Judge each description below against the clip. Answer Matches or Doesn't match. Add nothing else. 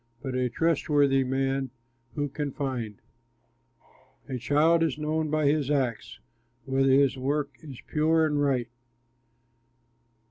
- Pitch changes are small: Matches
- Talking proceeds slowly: Matches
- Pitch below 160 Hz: Matches